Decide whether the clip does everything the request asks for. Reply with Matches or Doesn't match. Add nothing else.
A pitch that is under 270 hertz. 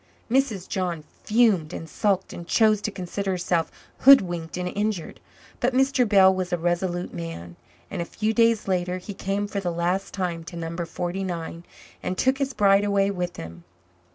Matches